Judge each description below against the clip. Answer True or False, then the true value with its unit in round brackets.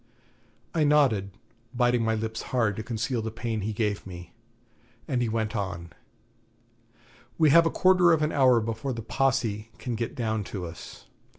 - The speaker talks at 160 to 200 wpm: True (170 wpm)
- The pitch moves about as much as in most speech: True (3.6 semitones)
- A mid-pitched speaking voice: False (115 Hz)